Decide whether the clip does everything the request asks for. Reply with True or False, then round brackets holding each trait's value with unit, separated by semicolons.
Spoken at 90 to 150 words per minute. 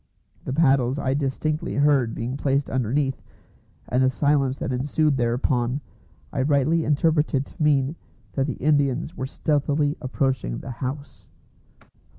True (135 wpm)